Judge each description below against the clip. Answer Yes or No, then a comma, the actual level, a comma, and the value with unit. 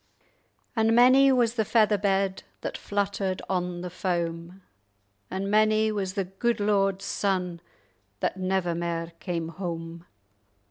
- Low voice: No, high, 190 Hz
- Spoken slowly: Yes, slow, 130 wpm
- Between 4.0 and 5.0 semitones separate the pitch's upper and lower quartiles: No, average, 3.1 semitones